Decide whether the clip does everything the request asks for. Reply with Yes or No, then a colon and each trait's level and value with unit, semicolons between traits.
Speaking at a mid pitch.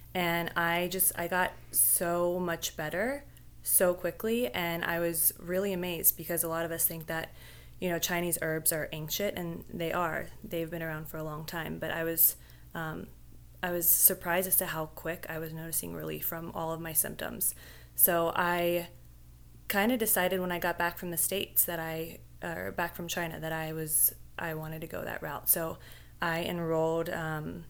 Yes: medium, 165 Hz